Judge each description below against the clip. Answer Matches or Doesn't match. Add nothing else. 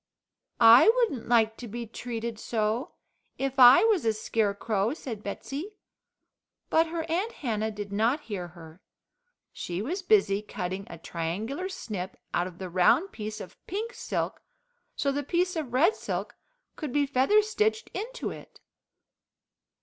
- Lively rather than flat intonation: Matches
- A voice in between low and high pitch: Doesn't match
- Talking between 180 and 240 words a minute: Doesn't match